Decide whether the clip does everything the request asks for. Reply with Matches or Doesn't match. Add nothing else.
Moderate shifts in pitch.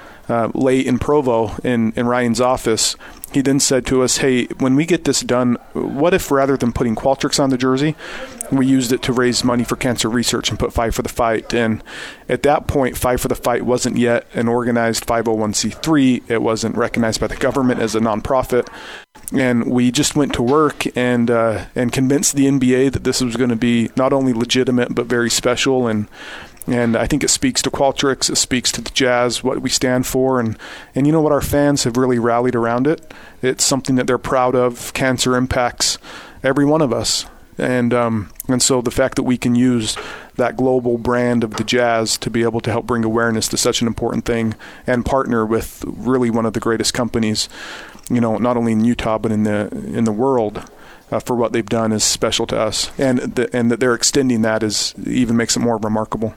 Doesn't match